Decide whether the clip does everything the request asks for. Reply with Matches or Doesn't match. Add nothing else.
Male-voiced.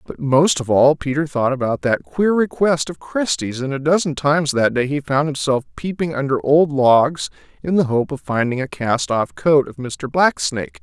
Matches